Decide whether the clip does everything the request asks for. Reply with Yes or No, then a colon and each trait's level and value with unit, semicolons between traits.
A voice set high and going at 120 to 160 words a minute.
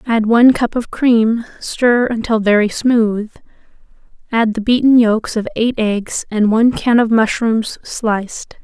Yes: high, 225 Hz; average, 155 wpm